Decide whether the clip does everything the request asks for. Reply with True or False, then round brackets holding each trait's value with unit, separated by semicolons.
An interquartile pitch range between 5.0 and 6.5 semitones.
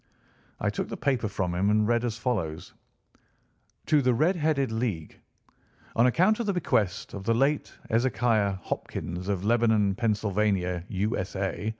False (4.2 semitones)